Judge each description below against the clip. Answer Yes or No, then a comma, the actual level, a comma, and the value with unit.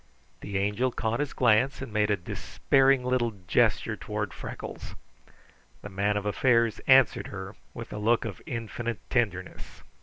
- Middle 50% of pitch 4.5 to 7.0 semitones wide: No, average, 3.4 semitones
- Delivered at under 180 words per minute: Yes, average, 150 wpm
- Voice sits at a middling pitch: No, low, 115 Hz